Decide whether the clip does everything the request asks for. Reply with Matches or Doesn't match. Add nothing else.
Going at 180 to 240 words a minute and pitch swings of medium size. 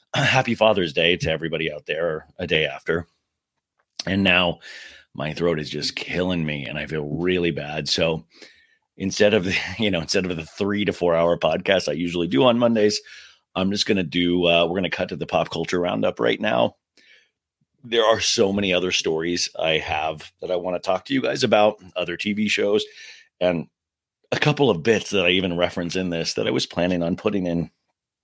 Matches